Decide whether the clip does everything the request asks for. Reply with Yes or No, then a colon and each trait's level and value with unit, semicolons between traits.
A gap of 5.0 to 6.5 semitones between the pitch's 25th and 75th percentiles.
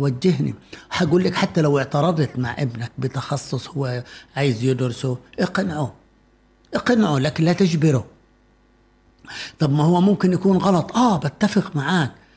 Yes: wide, 5.5 semitones